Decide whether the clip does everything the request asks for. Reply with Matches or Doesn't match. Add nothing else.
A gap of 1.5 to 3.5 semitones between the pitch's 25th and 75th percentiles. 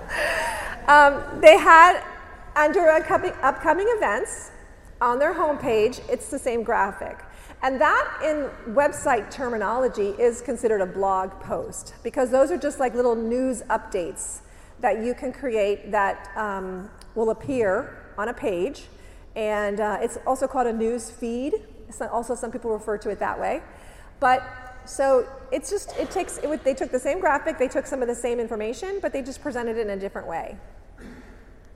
Doesn't match